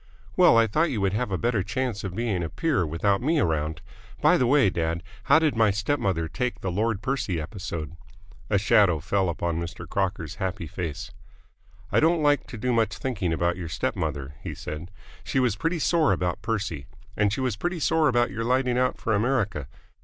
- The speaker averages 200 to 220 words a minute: Yes, fast, 205 wpm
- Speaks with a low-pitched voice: Yes, low, 105 Hz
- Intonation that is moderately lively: No, wide, 6.6 semitones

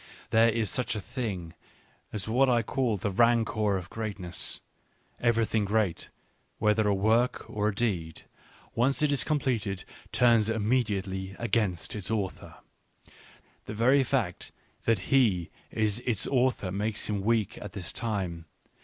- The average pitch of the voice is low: Yes, low, 110 Hz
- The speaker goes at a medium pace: Yes, average, 145 wpm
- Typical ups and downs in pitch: Yes, average, 3.1 semitones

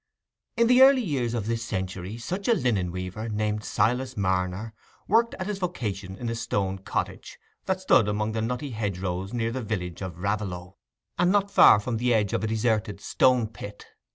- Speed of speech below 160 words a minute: No, average, 185 wpm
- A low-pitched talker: Yes, low, 110 Hz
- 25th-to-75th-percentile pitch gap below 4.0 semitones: No, average, 4.5 semitones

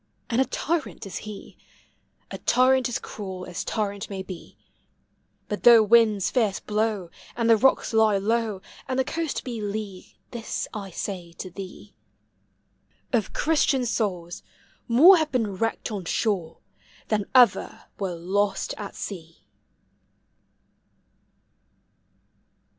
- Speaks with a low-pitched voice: No, high, 210 Hz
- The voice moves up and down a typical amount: Yes, average, 3.5 semitones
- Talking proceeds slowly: Yes, slow, 130 wpm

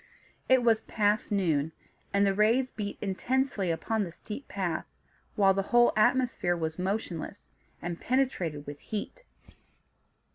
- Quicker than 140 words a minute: No, slow, 135 wpm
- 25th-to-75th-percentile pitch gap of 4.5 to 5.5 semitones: Yes, average, 4.9 semitones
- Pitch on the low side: No, high, 200 Hz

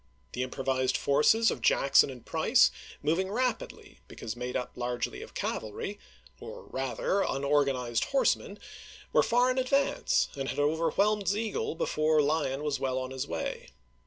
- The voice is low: No, medium, 145 Hz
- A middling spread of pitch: No, wide, 7.5 semitones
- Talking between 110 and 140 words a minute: No, average, 160 wpm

